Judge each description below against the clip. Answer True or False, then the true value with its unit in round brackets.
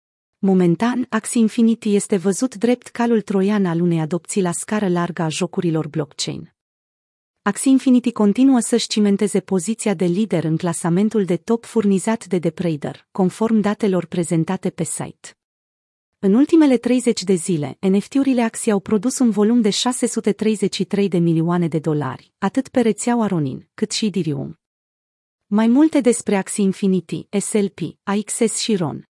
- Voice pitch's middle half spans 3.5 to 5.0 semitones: True (4.4 semitones)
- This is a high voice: True (200 Hz)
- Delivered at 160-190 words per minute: False (145 wpm)